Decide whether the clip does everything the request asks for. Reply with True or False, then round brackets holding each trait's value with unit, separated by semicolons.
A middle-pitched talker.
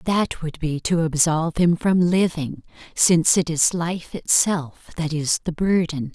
True (165 Hz)